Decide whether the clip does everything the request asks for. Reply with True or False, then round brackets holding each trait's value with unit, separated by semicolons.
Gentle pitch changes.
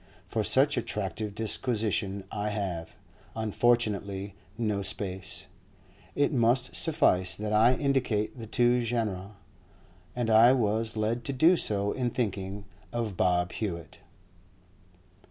False (3.3 semitones)